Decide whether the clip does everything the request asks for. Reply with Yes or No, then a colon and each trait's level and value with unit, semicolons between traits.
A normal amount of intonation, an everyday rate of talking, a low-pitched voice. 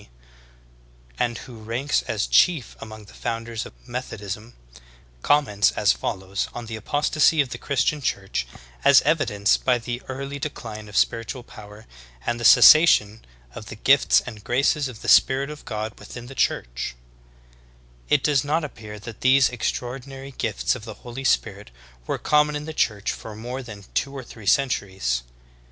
Yes: average, 4.4 semitones; average, 165 wpm; low, 120 Hz